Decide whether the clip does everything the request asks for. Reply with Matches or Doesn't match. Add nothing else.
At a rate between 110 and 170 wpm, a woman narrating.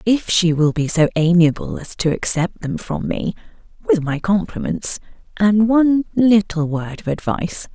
Matches